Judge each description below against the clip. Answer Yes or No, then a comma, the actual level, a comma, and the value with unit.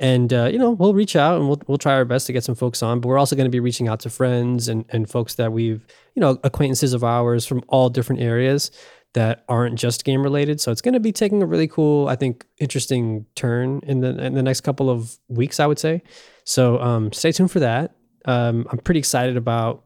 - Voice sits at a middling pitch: No, low, 130 Hz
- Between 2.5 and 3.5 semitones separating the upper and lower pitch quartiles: Yes, average, 3.0 semitones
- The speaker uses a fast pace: Yes, fast, 250 wpm